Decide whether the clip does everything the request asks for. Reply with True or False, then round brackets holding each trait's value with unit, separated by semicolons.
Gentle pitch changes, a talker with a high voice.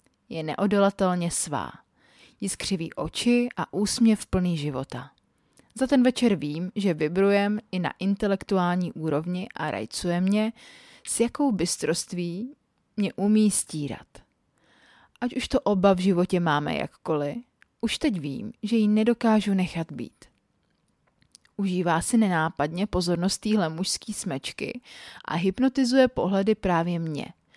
False (4.7 semitones; 195 Hz)